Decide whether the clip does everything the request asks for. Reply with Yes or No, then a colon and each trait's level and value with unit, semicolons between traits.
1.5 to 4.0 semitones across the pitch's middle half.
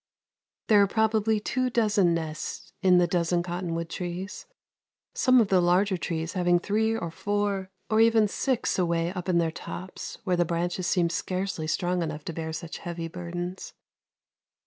Yes: average, 3.2 semitones